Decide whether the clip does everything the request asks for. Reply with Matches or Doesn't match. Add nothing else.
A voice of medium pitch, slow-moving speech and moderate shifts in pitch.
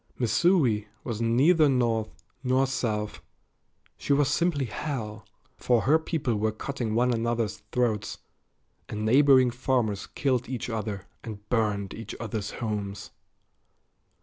Doesn't match